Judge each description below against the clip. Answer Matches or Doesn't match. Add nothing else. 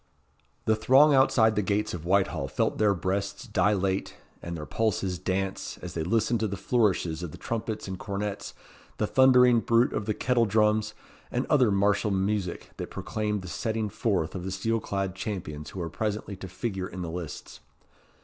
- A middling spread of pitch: Matches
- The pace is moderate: Matches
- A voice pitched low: Matches